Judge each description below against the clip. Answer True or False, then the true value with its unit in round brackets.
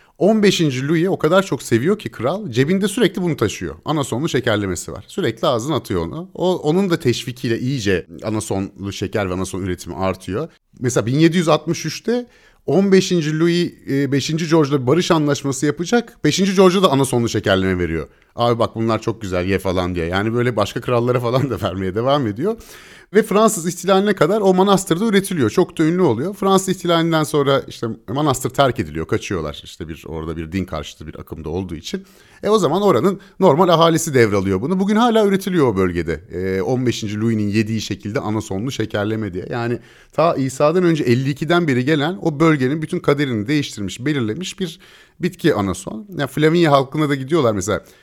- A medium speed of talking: False (165 wpm)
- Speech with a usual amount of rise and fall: False (8.7 semitones)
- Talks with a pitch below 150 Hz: True (140 Hz)